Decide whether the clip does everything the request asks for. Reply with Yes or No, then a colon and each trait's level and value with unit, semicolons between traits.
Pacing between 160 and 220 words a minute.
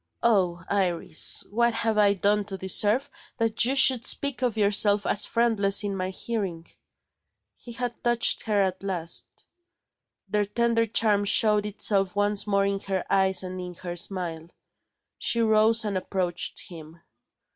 No: average, 150 wpm